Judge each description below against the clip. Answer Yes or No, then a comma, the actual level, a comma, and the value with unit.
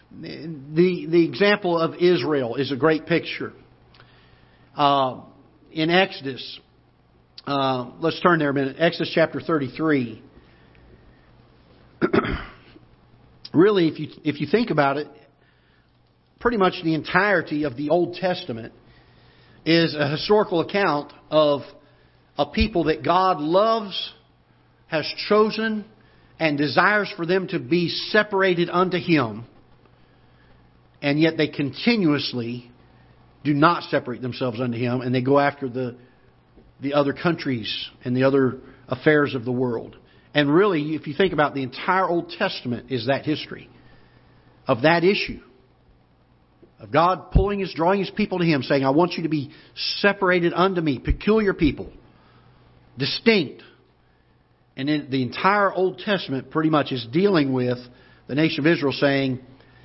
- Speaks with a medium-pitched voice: Yes, medium, 150 Hz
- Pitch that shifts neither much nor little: Yes, average, 4.9 semitones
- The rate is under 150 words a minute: Yes, slow, 135 wpm